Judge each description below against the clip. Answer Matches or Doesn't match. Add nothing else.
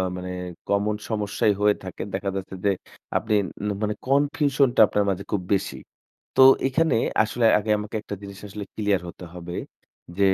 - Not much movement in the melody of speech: Matches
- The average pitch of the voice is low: Matches